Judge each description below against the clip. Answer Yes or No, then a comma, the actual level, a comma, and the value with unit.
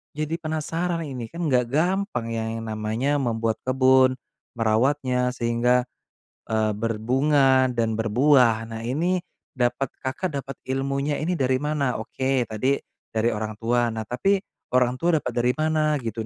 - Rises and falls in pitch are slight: No, average, 4.2 semitones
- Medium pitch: No, low, 130 Hz